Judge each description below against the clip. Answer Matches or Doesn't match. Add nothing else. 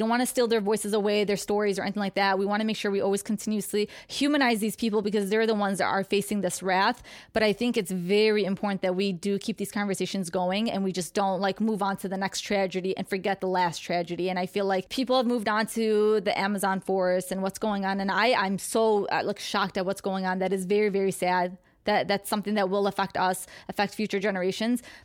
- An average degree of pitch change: Doesn't match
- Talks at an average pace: Doesn't match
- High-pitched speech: Matches